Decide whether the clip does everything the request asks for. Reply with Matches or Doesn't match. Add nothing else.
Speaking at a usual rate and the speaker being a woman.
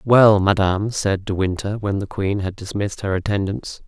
Doesn't match